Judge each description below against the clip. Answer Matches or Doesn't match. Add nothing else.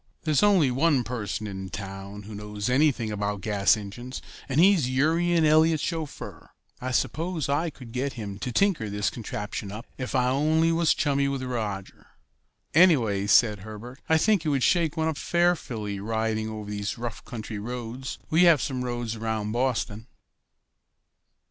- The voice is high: Doesn't match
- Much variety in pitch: Matches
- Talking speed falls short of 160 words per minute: Doesn't match